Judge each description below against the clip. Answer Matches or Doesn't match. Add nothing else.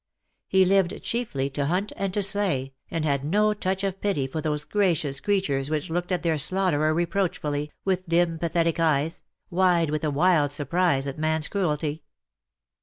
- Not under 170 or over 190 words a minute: Matches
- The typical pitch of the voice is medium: Matches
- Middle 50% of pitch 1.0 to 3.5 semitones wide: Doesn't match